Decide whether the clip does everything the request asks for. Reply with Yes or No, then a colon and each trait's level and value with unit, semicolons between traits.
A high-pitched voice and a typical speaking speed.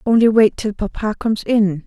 Yes: high, 215 Hz; average, 195 wpm